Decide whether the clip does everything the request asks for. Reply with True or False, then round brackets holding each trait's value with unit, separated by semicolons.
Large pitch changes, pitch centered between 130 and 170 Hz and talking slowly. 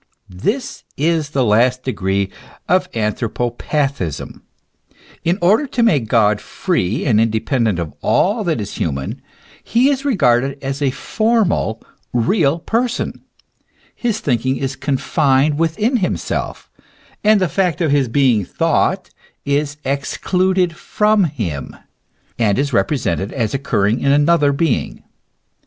True (7.8 semitones; 140 Hz; 125 wpm)